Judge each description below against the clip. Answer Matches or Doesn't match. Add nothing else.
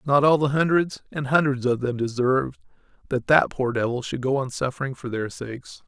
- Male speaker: Matches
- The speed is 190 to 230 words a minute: Matches